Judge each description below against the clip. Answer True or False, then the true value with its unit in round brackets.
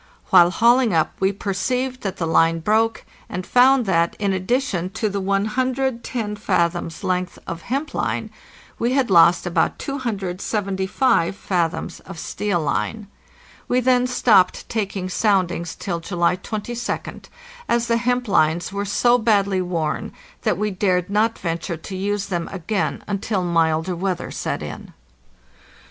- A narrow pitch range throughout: False (4.6 semitones)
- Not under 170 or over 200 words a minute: False (140 wpm)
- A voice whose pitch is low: False (195 Hz)